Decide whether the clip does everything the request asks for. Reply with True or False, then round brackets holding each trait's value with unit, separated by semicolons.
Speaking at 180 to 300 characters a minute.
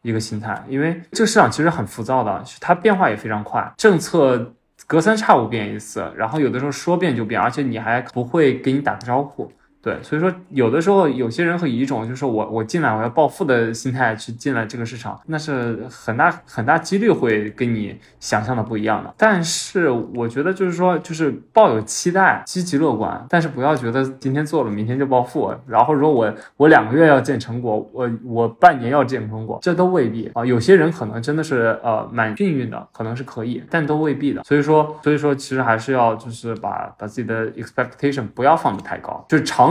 False (345 characters per minute)